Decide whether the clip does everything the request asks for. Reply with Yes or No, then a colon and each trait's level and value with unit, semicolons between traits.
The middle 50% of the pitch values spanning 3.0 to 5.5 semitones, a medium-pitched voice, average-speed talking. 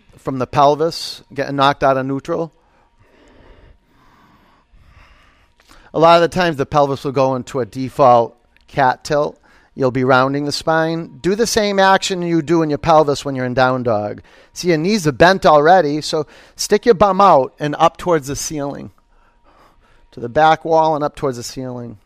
Yes: average, 4.0 semitones; medium, 145 Hz; average, 180 wpm